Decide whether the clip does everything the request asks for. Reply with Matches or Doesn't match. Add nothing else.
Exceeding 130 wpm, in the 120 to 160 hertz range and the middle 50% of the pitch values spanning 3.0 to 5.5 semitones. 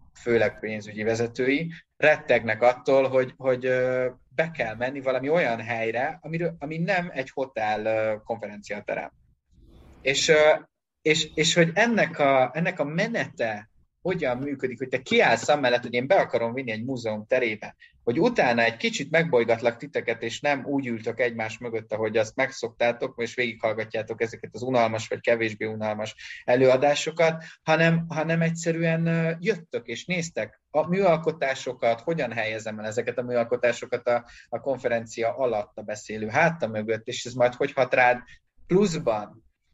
Matches